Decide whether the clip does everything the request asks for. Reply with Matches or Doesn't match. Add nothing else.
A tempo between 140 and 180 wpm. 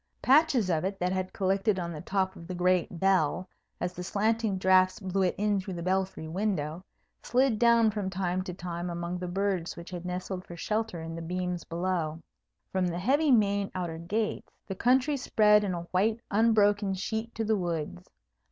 Doesn't match